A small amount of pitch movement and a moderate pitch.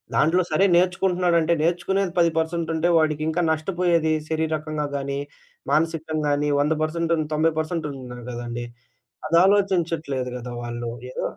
Yes: narrow, 2.3 semitones; medium, 160 Hz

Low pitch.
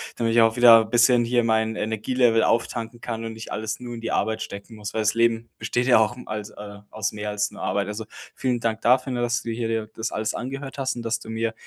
Yes: low, 115 Hz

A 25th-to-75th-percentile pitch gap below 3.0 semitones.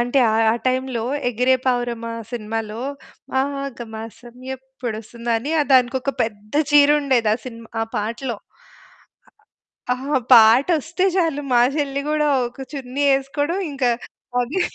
No: average, 3.3 semitones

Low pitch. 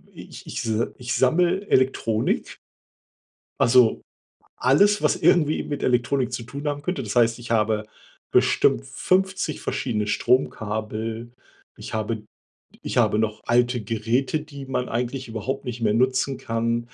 Yes: low, 120 Hz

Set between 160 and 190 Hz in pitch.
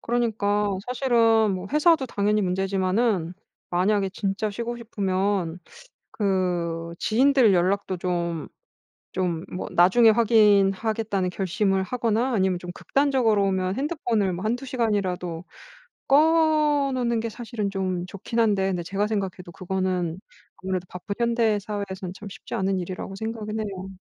No: high, 200 Hz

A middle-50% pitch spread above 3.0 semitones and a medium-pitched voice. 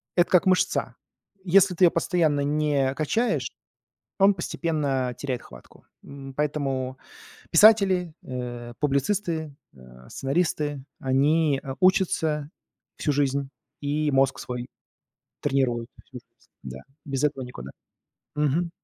Yes: average, 4.1 semitones; medium, 145 Hz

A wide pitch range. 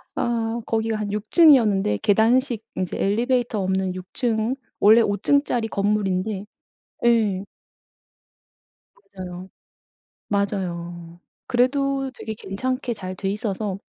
No: average, 3.7 semitones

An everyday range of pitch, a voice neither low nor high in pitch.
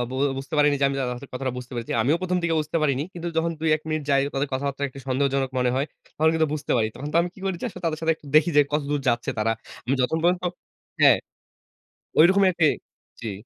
Yes: average, 3.6 semitones; medium, 145 Hz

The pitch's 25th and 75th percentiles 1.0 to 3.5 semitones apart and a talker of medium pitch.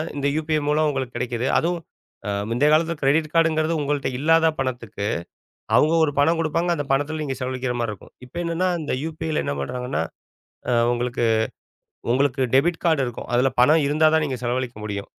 No: average, 4.1 semitones; medium, 145 Hz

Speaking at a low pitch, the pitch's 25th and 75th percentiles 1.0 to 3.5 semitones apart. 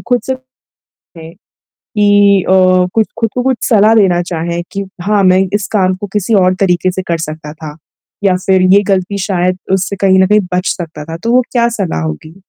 No: high, 190 Hz; average, 3.1 semitones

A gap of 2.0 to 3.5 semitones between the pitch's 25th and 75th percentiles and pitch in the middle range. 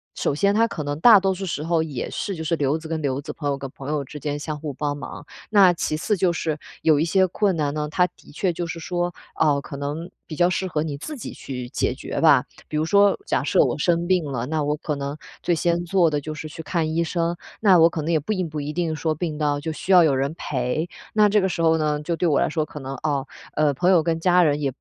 Yes: average, 3.1 semitones; medium, 160 Hz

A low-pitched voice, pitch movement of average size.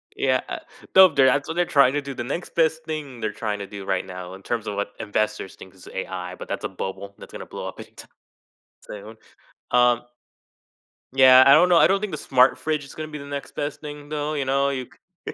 No: low, 130 Hz; wide, 6.2 semitones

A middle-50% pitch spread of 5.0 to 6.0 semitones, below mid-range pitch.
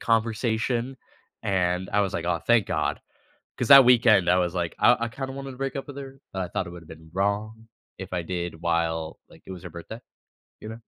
Yes: average, 5.3 semitones; low, 100 Hz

